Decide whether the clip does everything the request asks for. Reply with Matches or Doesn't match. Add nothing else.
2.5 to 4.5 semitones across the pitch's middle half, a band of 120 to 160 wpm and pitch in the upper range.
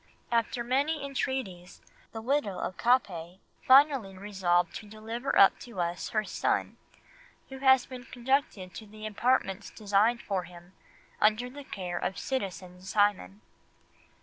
Doesn't match